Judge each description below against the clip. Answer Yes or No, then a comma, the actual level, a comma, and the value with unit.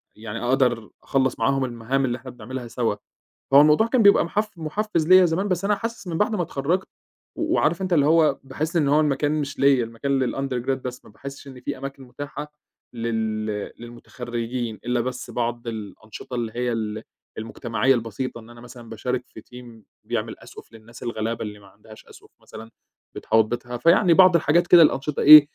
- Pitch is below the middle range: Yes, low, 130 Hz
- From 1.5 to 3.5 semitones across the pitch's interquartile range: No, average, 4.6 semitones